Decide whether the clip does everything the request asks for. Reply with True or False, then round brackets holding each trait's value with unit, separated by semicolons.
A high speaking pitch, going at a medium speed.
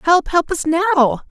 True (300 Hz; 185 wpm)